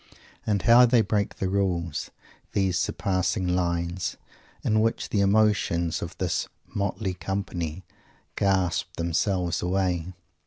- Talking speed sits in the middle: No, slow, 115 wpm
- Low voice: Yes, very low, 95 Hz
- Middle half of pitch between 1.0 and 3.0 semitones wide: Yes, narrow, 2.6 semitones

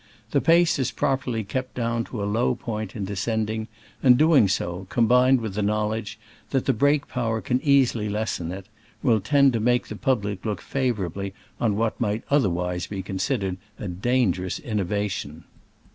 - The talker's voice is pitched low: Yes, low, 110 Hz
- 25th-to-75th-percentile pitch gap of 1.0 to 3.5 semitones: No, average, 4.0 semitones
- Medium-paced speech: Yes, average, 175 wpm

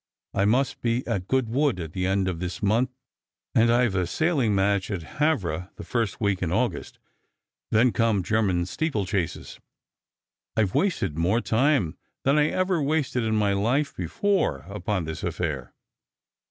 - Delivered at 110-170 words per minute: Yes, average, 155 wpm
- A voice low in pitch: Yes, low, 105 Hz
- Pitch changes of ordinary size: No, wide, 5.8 semitones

